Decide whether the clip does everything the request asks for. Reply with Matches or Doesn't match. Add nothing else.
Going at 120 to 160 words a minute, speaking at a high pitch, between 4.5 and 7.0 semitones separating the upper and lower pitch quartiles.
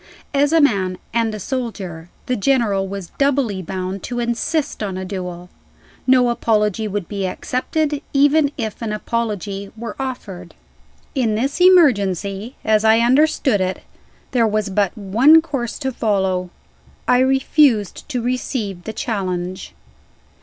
Matches